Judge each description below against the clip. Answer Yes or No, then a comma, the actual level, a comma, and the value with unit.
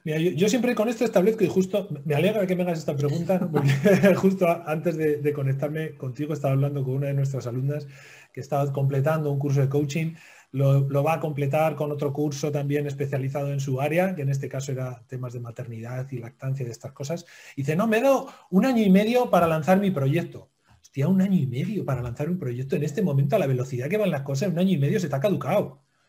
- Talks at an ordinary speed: No, fast, 240 wpm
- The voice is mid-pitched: Yes, medium, 150 Hz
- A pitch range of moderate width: Yes, average, 4.7 semitones